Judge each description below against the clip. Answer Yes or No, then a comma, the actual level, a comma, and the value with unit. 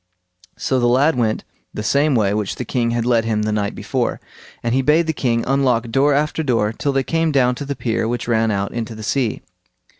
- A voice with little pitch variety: No, average, 3.5 semitones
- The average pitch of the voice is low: Yes, low, 120 Hz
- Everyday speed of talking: No, fast, 230 wpm